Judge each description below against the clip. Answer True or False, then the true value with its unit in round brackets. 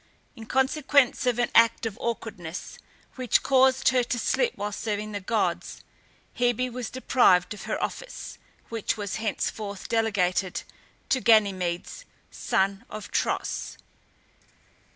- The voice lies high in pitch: True (225 Hz)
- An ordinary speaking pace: False (125 wpm)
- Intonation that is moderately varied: True (3.8 semitones)